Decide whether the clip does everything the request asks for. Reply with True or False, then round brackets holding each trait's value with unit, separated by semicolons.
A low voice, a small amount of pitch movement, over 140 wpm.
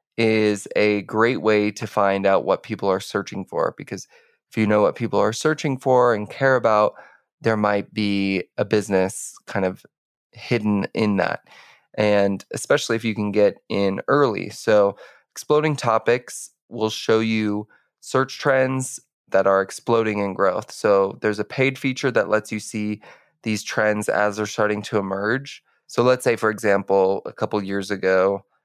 True (105 Hz; 2.3 semitones; 170 wpm)